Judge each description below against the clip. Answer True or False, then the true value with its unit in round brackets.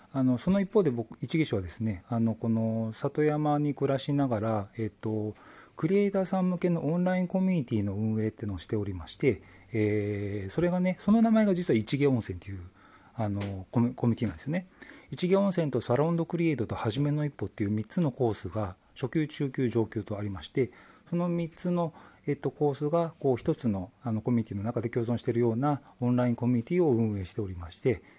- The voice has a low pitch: True (120 Hz)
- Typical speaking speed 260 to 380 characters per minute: False (415 characters per minute)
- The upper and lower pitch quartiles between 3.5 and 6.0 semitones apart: False (6.5 semitones)